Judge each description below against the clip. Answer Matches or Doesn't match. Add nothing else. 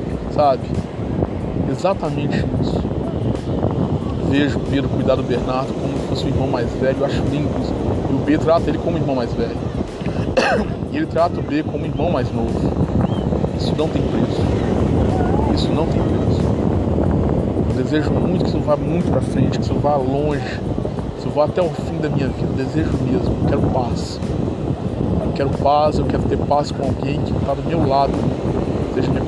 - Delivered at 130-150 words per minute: Doesn't match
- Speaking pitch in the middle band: Doesn't match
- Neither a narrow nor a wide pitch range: Matches